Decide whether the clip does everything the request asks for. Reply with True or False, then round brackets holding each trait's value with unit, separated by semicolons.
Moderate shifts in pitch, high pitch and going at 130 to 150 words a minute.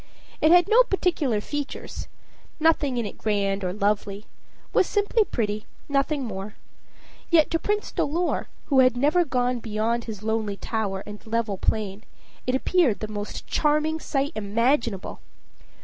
False (6.5 semitones; 235 Hz; 145 wpm)